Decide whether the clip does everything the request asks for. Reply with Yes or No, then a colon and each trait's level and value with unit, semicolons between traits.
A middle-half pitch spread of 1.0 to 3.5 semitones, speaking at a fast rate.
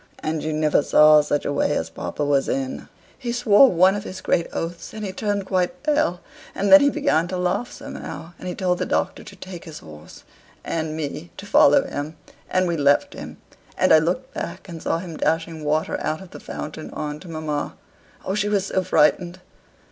No: average, 4.0 semitones; fast, 210 wpm